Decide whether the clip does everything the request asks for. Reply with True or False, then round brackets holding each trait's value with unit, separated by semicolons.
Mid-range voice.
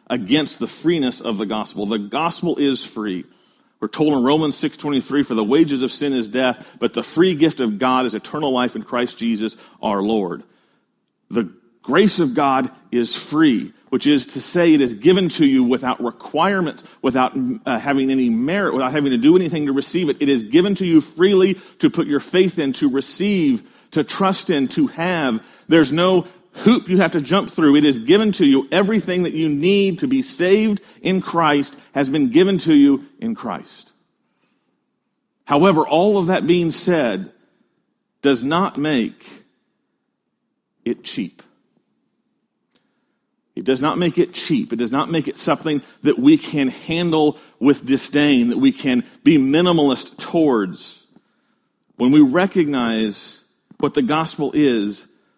True (160 Hz)